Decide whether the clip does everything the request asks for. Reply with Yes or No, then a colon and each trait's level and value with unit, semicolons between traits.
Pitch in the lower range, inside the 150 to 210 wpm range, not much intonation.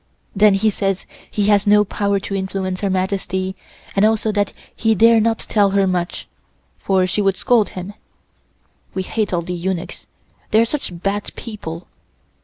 No: high, 195 Hz; average, 170 wpm; narrow, 2.1 semitones